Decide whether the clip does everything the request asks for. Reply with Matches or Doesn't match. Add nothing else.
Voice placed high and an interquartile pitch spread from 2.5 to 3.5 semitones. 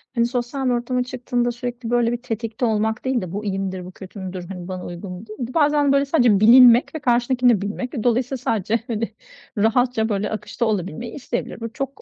Matches